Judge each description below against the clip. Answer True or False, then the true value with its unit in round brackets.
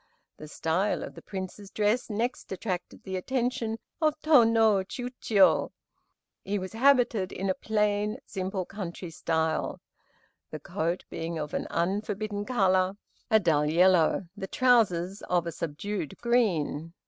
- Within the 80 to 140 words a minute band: True (135 wpm)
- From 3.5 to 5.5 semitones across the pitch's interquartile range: True (4.2 semitones)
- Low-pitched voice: False (195 Hz)